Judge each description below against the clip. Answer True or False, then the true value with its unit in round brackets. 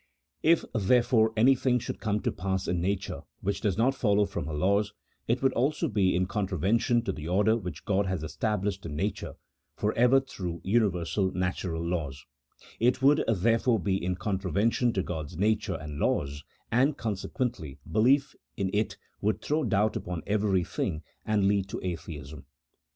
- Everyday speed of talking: True (165 wpm)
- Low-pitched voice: True (100 Hz)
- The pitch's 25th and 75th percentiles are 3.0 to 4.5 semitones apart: True (4.1 semitones)